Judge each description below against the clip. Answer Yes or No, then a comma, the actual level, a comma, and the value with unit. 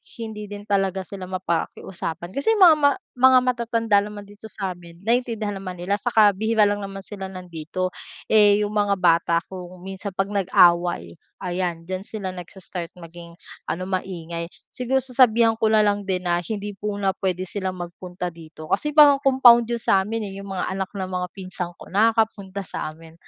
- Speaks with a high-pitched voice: Yes, high, 195 Hz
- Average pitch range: Yes, average, 3.2 semitones